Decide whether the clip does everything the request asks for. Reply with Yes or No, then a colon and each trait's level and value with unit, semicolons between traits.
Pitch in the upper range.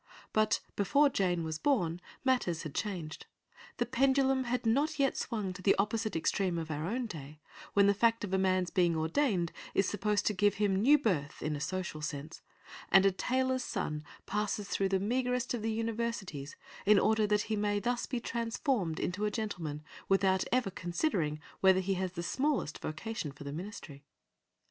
Yes: high, 200 Hz